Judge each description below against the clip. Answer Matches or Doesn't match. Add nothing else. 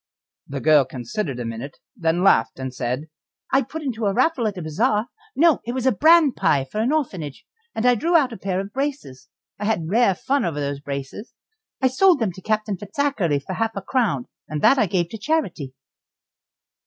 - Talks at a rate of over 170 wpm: Matches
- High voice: Matches